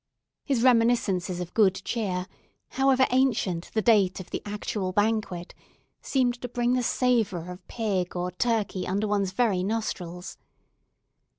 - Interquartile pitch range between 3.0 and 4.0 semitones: No, average, 4.7 semitones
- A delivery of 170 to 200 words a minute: No, slow, 135 wpm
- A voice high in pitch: Yes, high, 210 Hz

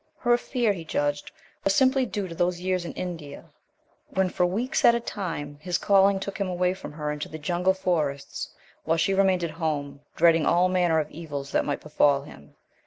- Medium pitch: Yes, medium, 175 Hz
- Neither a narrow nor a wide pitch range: Yes, average, 4.1 semitones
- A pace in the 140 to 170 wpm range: No, average, 200 wpm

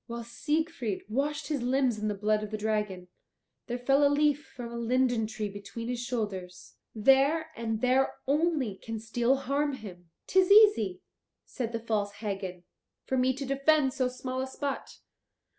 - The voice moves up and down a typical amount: Yes, average, 4.3 semitones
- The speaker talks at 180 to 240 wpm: No, average, 170 wpm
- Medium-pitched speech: No, high, 245 Hz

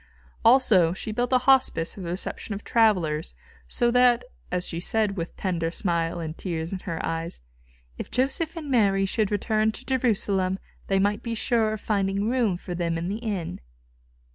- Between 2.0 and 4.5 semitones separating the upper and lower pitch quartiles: No, average, 5.0 semitones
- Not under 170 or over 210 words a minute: Yes, average, 175 wpm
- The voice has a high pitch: Yes, high, 200 Hz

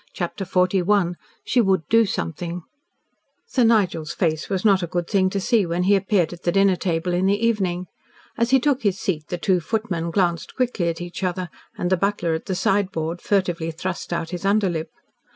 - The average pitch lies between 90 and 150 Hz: No, medium, 185 Hz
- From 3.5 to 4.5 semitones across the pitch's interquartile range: No, average, 2.8 semitones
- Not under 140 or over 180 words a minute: No, average, 195 wpm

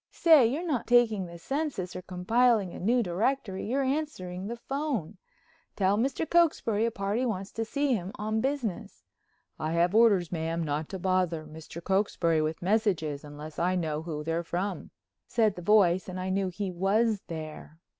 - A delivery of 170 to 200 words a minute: Yes, average, 175 wpm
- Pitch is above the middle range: Yes, high, 195 Hz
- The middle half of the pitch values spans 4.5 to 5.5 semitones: Yes, average, 5.2 semitones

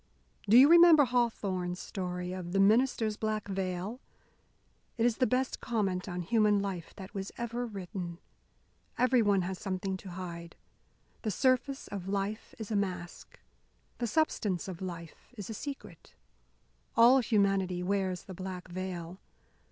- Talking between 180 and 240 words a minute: No, average, 145 wpm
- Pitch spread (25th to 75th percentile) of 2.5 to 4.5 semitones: Yes, average, 4.0 semitones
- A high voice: Yes, high, 195 Hz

